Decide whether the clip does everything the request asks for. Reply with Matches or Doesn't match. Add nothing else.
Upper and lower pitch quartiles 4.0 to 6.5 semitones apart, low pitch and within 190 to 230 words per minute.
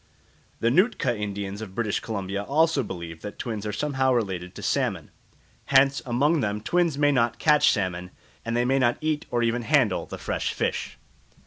Doesn't match